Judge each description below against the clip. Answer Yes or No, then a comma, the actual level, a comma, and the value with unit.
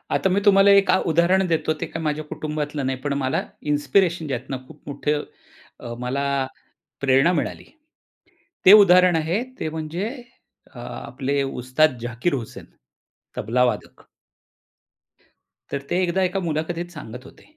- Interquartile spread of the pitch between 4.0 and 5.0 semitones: Yes, average, 4.4 semitones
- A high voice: No, medium, 155 Hz